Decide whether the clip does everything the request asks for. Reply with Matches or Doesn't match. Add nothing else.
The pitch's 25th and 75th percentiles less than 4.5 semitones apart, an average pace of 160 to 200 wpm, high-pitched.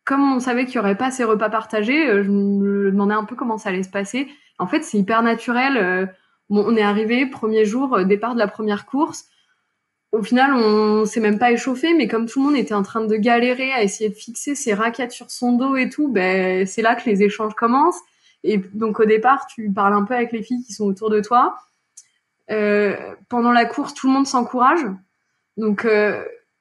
Doesn't match